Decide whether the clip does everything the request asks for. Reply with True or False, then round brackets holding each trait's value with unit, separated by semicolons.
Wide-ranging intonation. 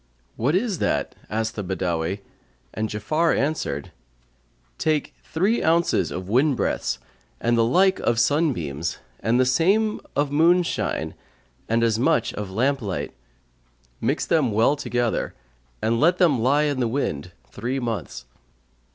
True (6.6 semitones)